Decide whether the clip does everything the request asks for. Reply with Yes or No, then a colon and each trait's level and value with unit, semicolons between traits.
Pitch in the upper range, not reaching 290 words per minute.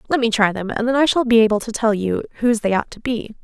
No: high, 230 Hz; fast, 315 wpm